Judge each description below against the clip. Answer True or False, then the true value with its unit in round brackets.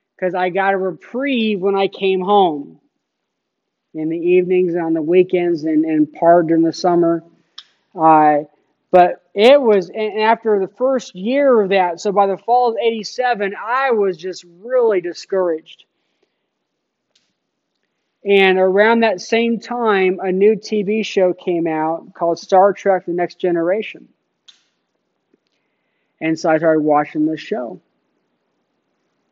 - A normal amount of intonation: True (4.1 semitones)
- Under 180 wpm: True (140 wpm)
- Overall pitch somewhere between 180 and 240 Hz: True (185 Hz)